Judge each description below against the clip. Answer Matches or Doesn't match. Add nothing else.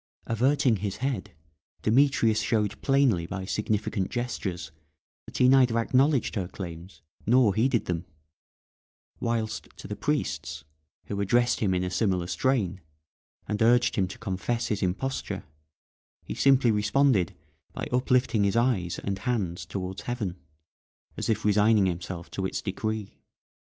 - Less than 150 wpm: Matches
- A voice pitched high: Doesn't match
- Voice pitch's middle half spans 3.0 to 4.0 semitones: Doesn't match